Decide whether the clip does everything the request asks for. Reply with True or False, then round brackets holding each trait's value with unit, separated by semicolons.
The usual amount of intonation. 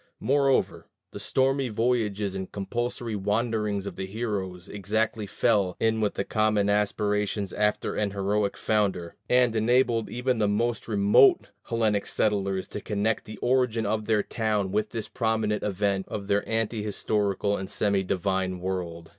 False (2.2 semitones)